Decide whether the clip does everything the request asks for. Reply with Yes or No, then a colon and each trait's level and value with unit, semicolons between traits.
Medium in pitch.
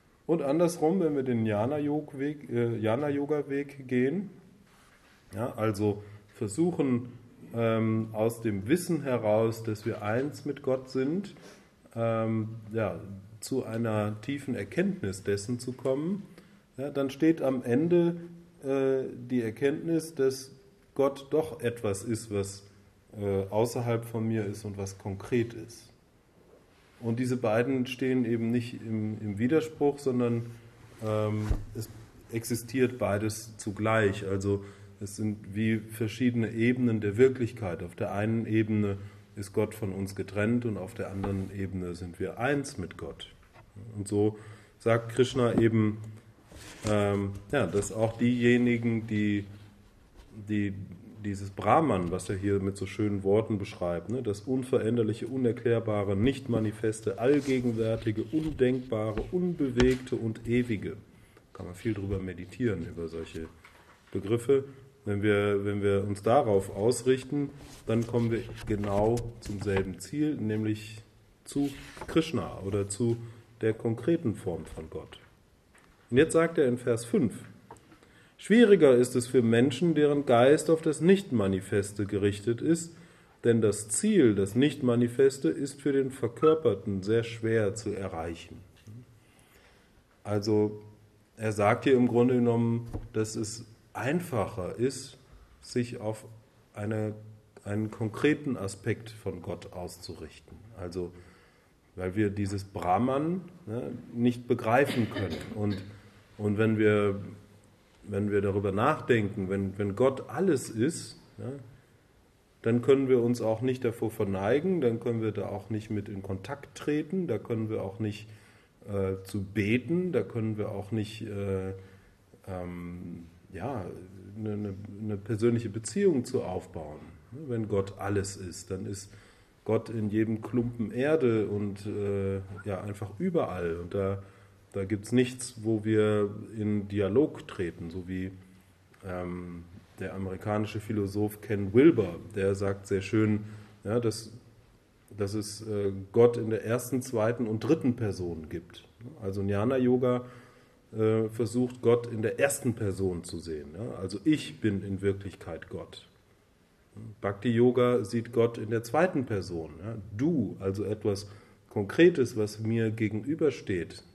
No: low, 110 Hz